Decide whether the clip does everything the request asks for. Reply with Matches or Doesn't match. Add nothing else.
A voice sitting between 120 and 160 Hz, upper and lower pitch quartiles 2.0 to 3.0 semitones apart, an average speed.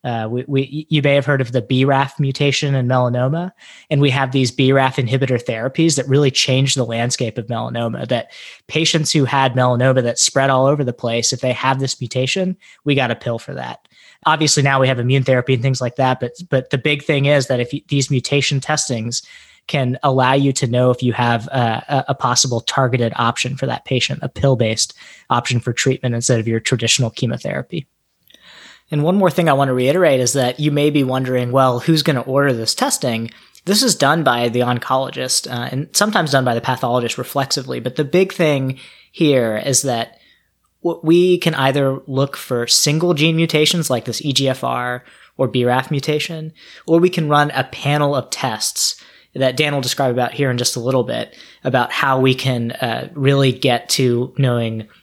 Matches